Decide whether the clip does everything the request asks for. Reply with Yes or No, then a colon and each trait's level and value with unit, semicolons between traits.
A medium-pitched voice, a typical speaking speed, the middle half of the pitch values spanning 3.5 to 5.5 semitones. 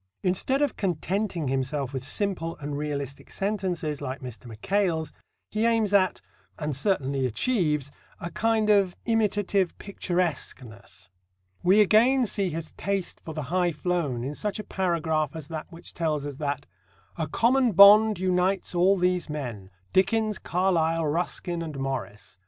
Yes: medium, 175 Hz; average, 145 wpm; average, 5.2 semitones